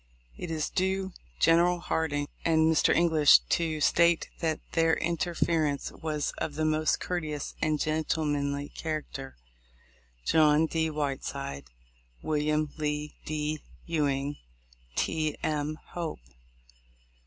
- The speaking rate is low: Yes, slow, 110 wpm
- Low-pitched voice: No, medium, 155 Hz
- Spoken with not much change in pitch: Yes, narrow, 1.6 semitones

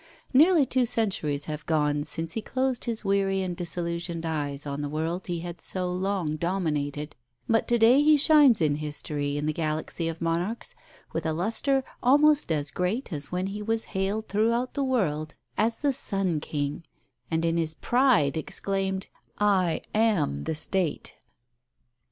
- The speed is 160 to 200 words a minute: Yes, average, 165 wpm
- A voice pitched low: No, medium, 180 Hz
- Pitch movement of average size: No, wide, 6.4 semitones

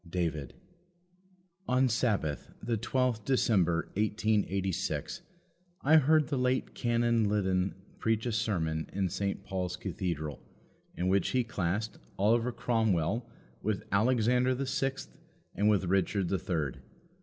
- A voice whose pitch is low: Yes, low, 105 Hz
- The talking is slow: Yes, slow, 120 wpm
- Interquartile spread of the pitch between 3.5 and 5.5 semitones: Yes, average, 4.6 semitones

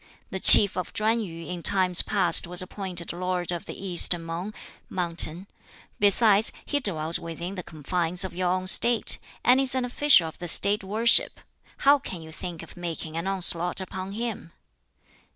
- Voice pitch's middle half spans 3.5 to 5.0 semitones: No, average, 3.1 semitones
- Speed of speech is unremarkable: Yes, average, 170 wpm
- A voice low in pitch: No, medium, 185 Hz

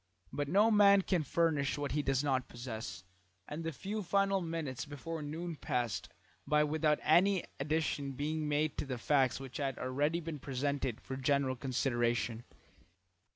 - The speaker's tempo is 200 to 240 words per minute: No, average, 155 wpm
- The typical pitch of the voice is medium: Yes, medium, 145 Hz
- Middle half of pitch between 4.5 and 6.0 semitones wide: No, average, 3.7 semitones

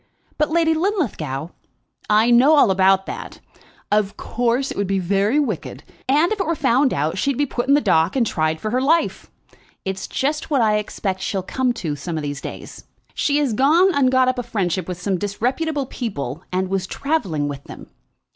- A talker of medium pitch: No, high, 225 Hz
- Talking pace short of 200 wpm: No, fast, 205 wpm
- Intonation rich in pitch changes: Yes, wide, 7.0 semitones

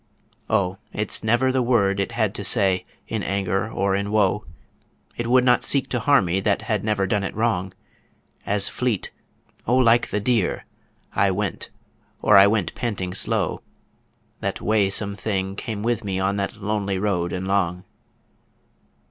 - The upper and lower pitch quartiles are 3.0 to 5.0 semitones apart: No, narrow, 2.5 semitones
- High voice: No, low, 100 Hz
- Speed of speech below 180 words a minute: Yes, average, 165 wpm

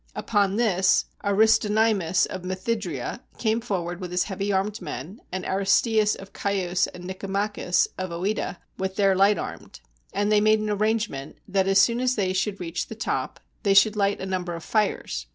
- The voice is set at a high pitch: Yes, high, 195 Hz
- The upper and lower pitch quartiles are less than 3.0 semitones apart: Yes, narrow, 2.4 semitones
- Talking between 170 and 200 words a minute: Yes, average, 175 wpm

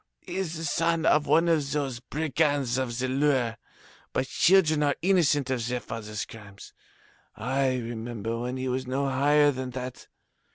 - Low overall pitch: Yes, low, 130 Hz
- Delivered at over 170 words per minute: No, average, 165 wpm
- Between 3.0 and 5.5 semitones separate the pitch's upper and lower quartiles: Yes, average, 3.4 semitones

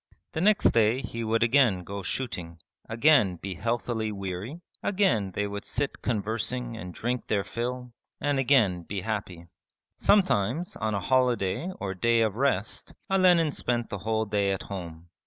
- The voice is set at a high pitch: No, low, 110 Hz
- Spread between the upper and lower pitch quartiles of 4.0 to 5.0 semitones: Yes, average, 4.4 semitones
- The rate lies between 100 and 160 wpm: Yes, average, 155 wpm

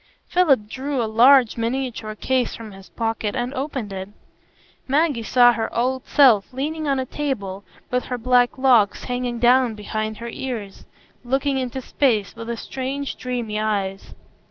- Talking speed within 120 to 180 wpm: Yes, average, 155 wpm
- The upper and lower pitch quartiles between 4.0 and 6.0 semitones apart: No, average, 3.3 semitones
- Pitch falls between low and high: No, high, 245 Hz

